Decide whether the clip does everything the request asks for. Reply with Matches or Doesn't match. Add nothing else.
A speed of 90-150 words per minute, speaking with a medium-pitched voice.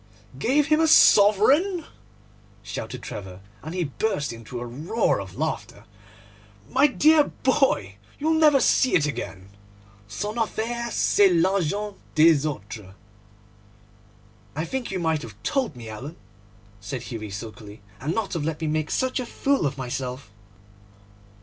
Matches